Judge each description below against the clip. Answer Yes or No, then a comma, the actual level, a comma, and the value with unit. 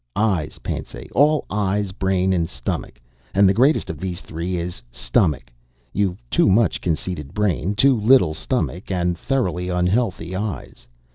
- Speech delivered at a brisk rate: No, average, 145 wpm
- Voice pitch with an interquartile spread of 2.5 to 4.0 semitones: Yes, average, 3.6 semitones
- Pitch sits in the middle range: No, very low, 95 Hz